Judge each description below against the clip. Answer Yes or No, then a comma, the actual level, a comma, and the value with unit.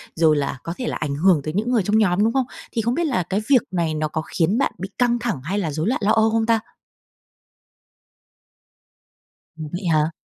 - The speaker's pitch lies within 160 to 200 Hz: Yes, high, 190 Hz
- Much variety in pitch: Yes, wide, 6.1 semitones